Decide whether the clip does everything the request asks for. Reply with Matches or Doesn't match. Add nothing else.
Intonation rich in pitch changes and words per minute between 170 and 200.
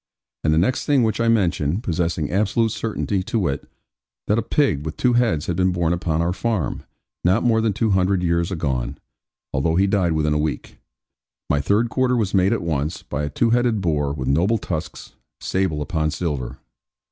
Matches